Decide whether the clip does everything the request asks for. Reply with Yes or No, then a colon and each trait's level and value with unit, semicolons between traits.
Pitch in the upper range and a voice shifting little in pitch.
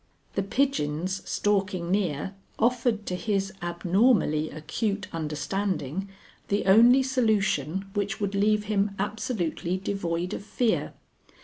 No: high, 195 Hz; average, 3.5 semitones